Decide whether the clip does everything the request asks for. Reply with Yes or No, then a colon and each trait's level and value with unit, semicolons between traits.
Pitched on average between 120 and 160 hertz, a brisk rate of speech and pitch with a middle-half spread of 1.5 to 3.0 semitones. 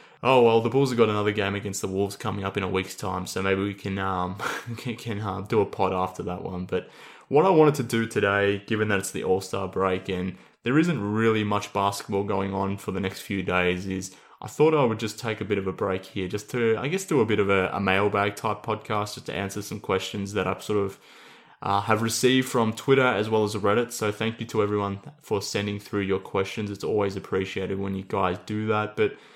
No: low, 100 Hz; fast, 245 wpm; narrow, 2.6 semitones